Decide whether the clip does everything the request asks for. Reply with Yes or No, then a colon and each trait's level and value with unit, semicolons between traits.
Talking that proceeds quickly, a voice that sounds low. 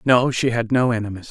Yes: fast, 230 wpm; low, 120 Hz